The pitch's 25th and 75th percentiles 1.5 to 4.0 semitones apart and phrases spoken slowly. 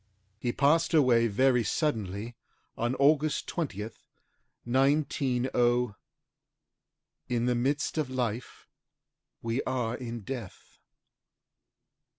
Yes: average, 2.9 semitones; slow, 90 wpm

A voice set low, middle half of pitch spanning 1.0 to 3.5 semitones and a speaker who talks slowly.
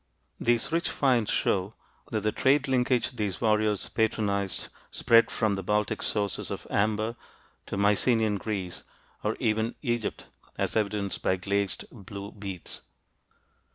Yes: low, 105 Hz; narrow, 2.5 semitones; slow, 130 wpm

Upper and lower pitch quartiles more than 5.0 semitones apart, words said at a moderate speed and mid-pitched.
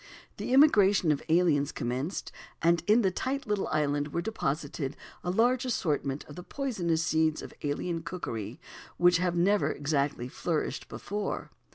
Yes: wide, 5.6 semitones; average, 150 wpm; medium, 170 Hz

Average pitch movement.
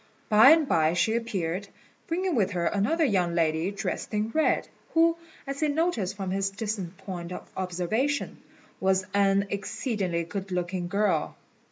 Yes: average, 4.4 semitones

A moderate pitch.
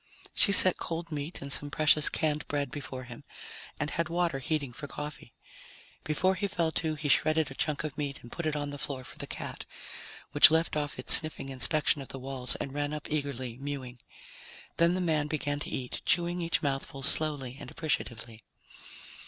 Yes: medium, 145 Hz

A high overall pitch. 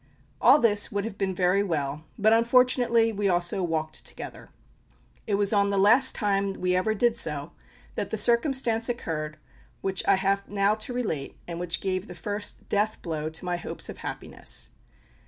Yes: high, 200 Hz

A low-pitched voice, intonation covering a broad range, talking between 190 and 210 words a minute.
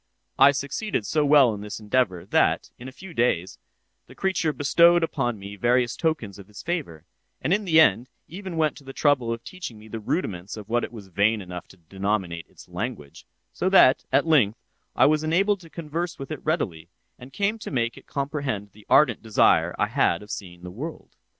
Yes: low, 125 Hz; wide, 7.6 semitones; fast, 205 wpm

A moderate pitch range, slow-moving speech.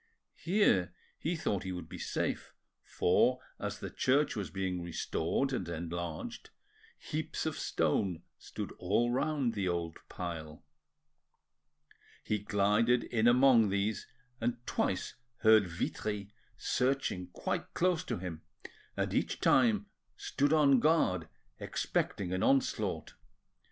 No: wide, 6.5 semitones; slow, 120 wpm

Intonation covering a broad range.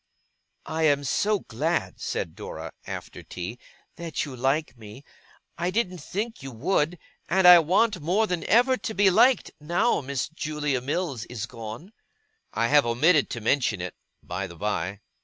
Yes: wide, 7.4 semitones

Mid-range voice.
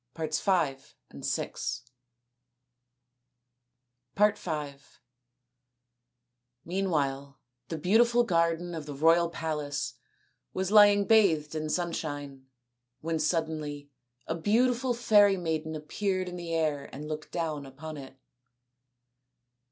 Yes: medium, 165 Hz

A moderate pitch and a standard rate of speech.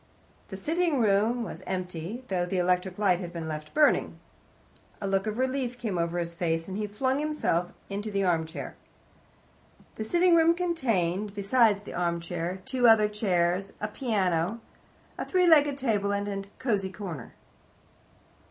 No: high, 200 Hz; average, 155 wpm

